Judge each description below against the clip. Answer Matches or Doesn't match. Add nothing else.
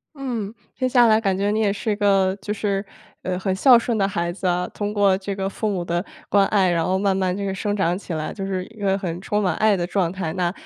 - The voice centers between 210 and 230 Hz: Doesn't match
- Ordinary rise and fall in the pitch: Doesn't match